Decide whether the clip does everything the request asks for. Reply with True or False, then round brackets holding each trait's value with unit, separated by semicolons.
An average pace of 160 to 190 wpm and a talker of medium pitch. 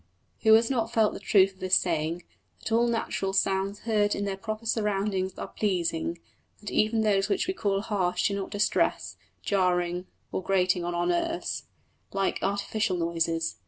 False (170 wpm; 195 Hz)